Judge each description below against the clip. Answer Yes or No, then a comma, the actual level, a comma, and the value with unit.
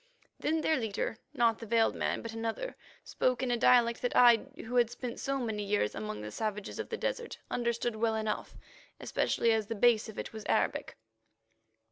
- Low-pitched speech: No, high, 230 Hz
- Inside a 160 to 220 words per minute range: Yes, average, 180 wpm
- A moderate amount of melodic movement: No, narrow, 1.9 semitones